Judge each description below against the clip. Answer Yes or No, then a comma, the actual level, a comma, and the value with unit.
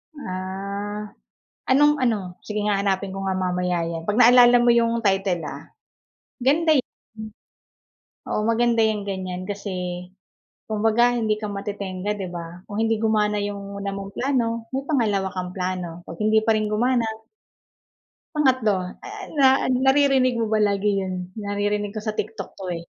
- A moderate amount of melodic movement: Yes, average, 3.3 semitones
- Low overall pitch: No, high, 210 Hz